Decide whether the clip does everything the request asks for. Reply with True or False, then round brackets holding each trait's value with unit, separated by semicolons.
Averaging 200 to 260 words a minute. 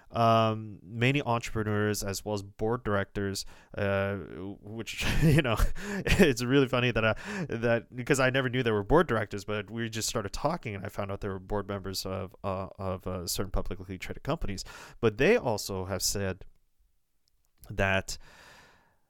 False (165 wpm)